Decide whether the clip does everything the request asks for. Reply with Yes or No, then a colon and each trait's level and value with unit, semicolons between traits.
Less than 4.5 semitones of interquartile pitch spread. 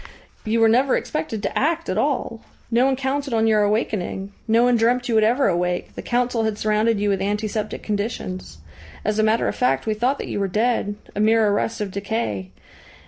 Yes: average, 2.8 semitones